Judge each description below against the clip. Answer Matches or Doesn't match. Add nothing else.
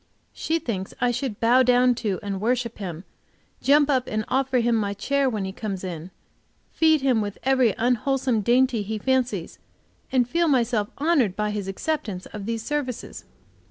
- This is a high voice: Matches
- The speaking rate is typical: Matches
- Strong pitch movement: Doesn't match